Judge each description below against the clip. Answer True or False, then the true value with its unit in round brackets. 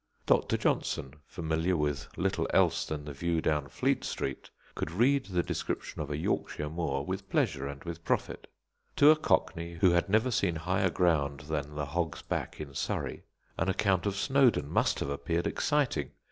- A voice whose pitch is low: True (85 Hz)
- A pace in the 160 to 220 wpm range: True (175 wpm)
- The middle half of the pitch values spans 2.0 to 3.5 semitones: False (4.2 semitones)